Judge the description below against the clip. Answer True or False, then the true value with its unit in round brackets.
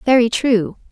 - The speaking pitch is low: False (235 Hz)